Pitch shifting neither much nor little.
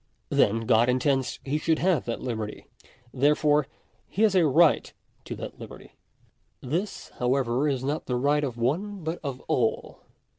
Yes: average, 4.0 semitones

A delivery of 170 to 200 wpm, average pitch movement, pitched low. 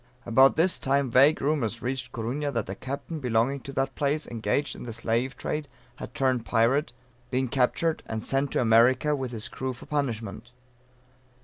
Yes: average, 175 wpm; average, 3.2 semitones; low, 130 Hz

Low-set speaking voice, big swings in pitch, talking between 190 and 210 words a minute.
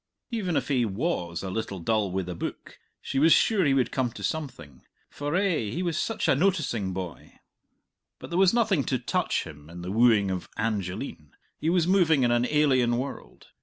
Yes: low, 125 Hz; wide, 8.9 semitones; average, 200 wpm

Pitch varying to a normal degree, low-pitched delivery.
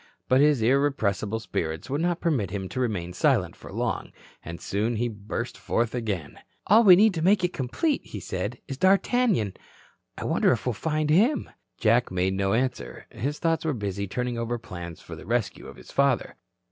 No: wide, 7.2 semitones; low, 120 Hz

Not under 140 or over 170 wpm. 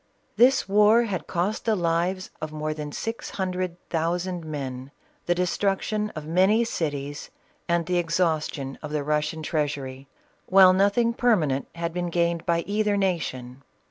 Yes: average, 150 wpm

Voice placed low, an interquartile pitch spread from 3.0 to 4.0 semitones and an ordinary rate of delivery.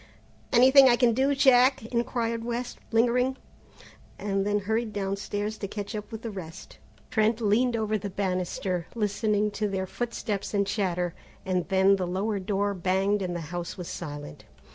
No: high, 205 Hz; average, 3.4 semitones; average, 165 wpm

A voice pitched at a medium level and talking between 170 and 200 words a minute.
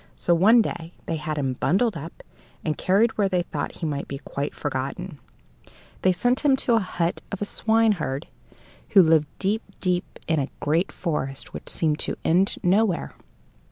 Yes: medium, 175 Hz; average, 175 wpm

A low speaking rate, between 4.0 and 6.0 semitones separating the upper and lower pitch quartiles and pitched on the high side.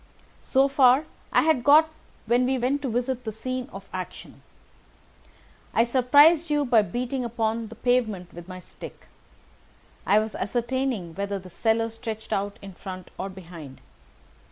No: average, 155 wpm; average, 4.5 semitones; high, 230 Hz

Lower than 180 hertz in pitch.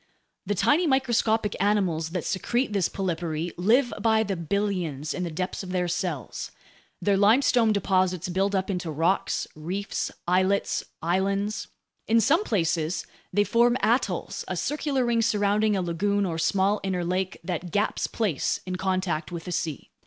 No: high, 190 Hz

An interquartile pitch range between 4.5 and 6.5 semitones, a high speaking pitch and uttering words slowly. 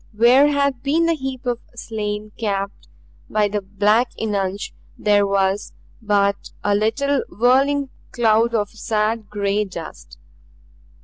No: average, 3.4 semitones; high, 215 Hz; slow, 125 wpm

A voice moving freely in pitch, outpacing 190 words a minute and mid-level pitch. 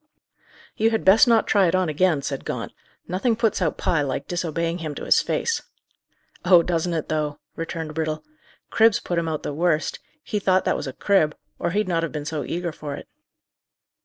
No: average, 3.3 semitones; average, 200 wpm; medium, 170 Hz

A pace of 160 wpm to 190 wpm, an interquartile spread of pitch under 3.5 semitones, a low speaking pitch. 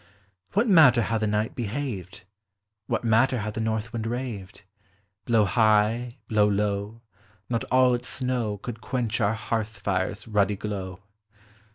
No: average, 145 wpm; average, 2.7 semitones; low, 110 Hz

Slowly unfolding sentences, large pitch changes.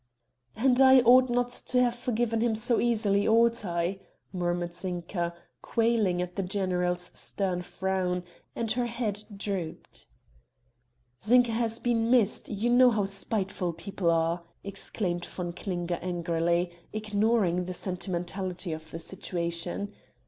No: slow, 130 wpm; average, 4.5 semitones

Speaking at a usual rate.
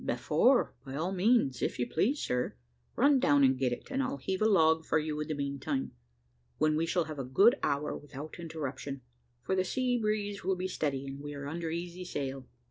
No: fast, 210 wpm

